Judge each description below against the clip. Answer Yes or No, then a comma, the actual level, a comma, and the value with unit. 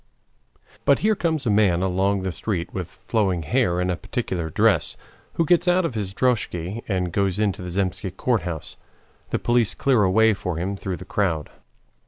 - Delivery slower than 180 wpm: No, average, 195 wpm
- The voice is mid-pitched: No, very low, 95 Hz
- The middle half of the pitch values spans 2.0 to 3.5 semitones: No, average, 4.1 semitones